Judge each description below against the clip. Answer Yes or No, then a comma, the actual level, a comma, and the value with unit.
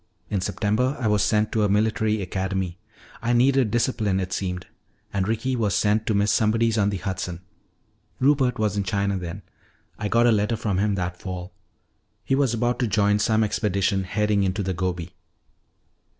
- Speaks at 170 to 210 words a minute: Yes, average, 180 wpm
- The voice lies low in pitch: Yes, low, 105 Hz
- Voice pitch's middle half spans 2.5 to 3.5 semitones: Yes, average, 2.9 semitones